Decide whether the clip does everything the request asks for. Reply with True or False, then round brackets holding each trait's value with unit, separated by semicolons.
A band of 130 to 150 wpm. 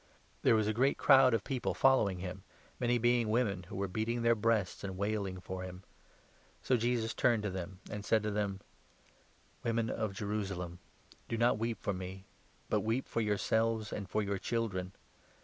False (170 wpm)